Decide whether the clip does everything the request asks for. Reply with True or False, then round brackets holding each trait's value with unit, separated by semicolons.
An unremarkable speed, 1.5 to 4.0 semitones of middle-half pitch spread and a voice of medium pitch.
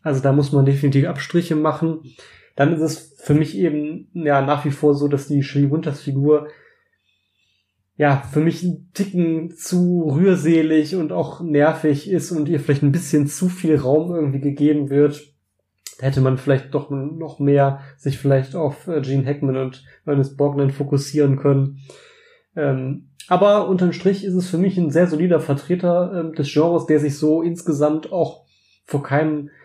True (160 wpm; 2.8 semitones; 150 Hz)